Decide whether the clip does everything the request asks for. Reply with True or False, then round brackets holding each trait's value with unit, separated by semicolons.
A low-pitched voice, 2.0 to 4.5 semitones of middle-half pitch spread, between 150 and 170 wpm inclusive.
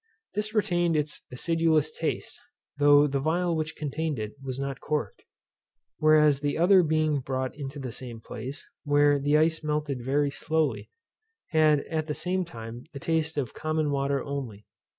False (150 Hz; 2.5 semitones; 160 wpm)